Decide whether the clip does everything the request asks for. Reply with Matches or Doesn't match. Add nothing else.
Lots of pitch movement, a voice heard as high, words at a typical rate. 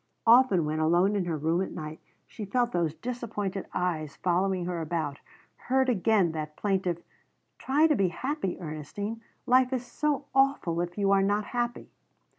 Matches